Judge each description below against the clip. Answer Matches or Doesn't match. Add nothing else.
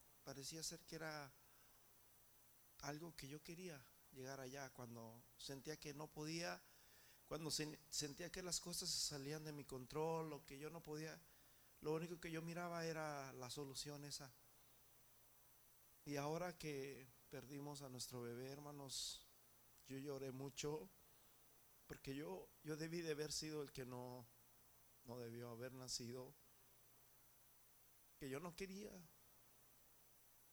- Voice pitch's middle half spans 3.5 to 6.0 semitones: Doesn't match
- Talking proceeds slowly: Doesn't match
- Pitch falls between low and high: Matches